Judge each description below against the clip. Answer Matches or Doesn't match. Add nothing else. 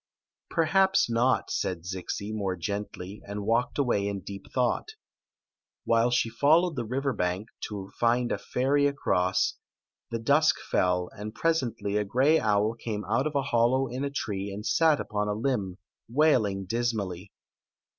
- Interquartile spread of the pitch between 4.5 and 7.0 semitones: Matches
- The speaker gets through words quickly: Doesn't match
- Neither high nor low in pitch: Doesn't match